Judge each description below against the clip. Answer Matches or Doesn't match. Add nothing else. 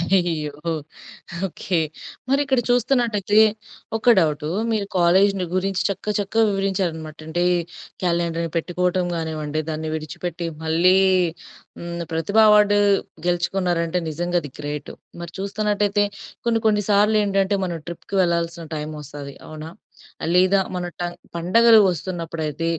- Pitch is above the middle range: Doesn't match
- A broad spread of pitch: Doesn't match